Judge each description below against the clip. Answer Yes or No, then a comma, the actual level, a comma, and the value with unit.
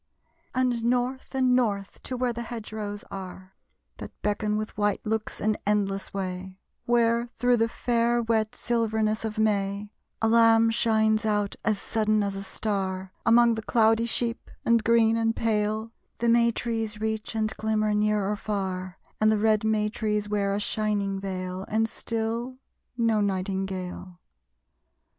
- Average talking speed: Yes, average, 155 wpm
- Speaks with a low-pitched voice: No, high, 215 Hz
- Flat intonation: Yes, narrow, 2.1 semitones